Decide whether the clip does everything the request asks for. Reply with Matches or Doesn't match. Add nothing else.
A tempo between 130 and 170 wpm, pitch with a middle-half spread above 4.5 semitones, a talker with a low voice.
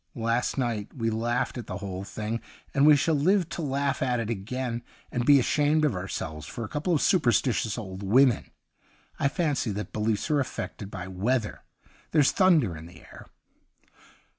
Doesn't match